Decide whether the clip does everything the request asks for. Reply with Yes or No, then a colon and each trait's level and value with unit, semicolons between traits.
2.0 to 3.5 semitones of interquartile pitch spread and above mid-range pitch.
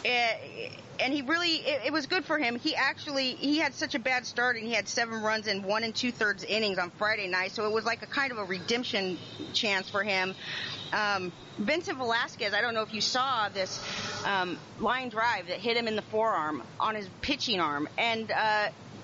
No: average, 3.9 semitones; high, 220 Hz